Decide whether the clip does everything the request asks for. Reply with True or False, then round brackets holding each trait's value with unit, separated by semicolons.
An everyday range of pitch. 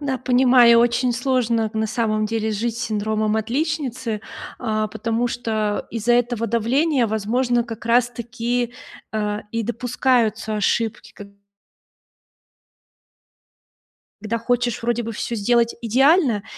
False (2.1 semitones)